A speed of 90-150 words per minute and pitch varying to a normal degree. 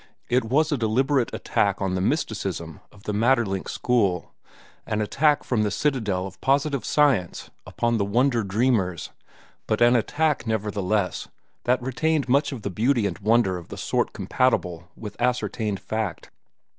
Yes: average, 145 wpm; average, 4.6 semitones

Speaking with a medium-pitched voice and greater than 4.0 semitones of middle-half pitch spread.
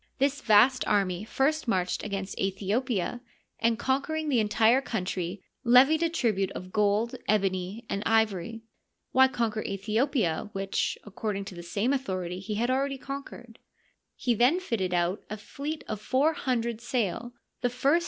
No: high, 225 Hz; average, 4.8 semitones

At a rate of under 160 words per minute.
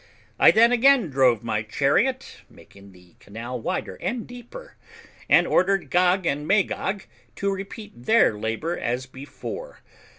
Yes: slow, 135 wpm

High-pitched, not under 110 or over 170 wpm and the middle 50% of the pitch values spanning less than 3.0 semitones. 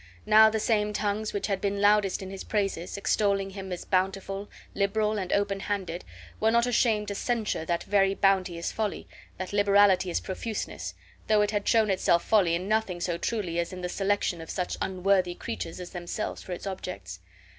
No: high, 195 Hz; average, 190 wpm; narrow, 2.4 semitones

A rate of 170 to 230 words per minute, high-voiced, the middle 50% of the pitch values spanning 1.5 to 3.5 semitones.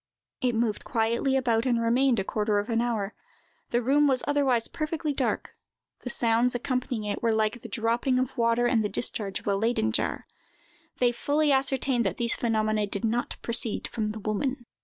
Yes: average, 185 wpm; high, 235 Hz; average, 2.7 semitones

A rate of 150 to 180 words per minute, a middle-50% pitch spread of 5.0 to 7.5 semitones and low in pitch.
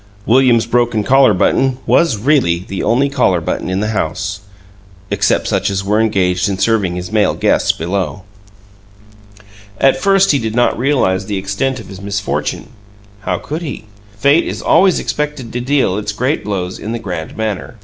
Yes: average, 170 wpm; wide, 5.4 semitones; low, 110 Hz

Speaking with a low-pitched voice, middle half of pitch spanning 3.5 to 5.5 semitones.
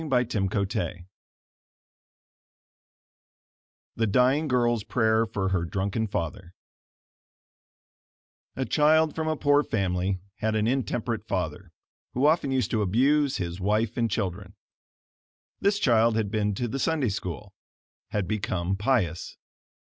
Yes: low, 110 Hz; average, 5.0 semitones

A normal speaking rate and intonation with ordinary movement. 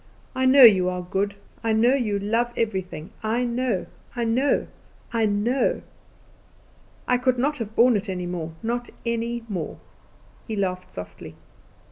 Yes: average, 150 wpm; average, 4.0 semitones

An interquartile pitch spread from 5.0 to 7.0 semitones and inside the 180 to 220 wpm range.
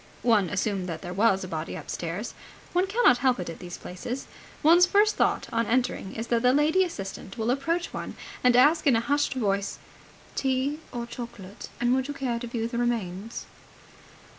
Yes: wide, 5.6 semitones; average, 190 wpm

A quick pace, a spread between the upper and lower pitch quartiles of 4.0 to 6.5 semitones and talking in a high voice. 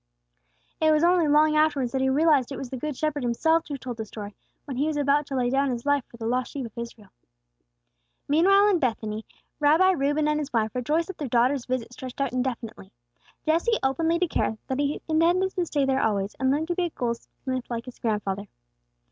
Yes: fast, 215 wpm; average, 4.3 semitones; very high, 275 Hz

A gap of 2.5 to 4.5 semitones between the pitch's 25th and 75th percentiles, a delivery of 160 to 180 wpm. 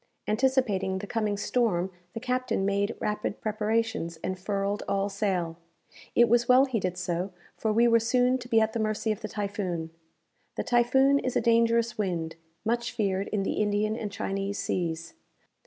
Yes: average, 3.2 semitones; average, 170 wpm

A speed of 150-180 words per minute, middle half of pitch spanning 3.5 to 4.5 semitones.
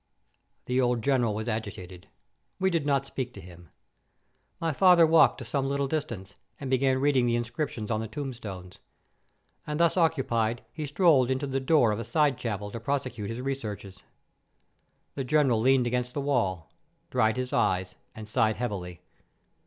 Yes: average, 165 wpm; average, 4.2 semitones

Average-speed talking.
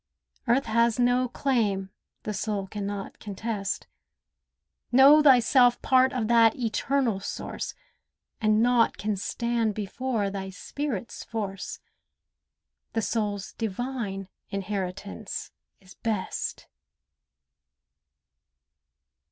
No: slow, 95 wpm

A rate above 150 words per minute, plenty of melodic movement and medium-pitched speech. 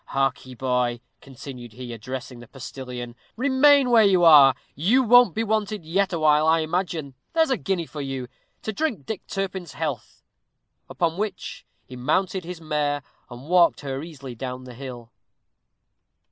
Yes: average, 160 wpm; wide, 7.0 semitones; medium, 155 Hz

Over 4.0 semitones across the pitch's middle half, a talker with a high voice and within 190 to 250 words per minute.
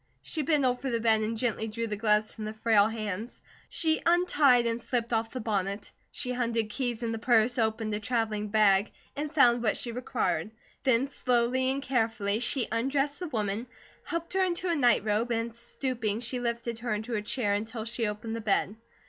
No: narrow, 2.6 semitones; high, 230 Hz; average, 200 wpm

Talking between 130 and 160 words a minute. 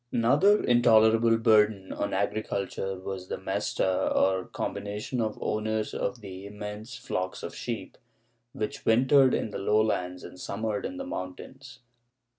Yes: average, 140 wpm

